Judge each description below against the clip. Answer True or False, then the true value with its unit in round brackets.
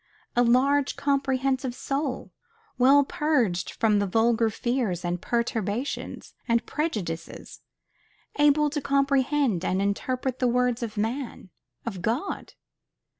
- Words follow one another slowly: True (110 wpm)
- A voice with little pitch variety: False (4.1 semitones)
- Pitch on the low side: False (250 Hz)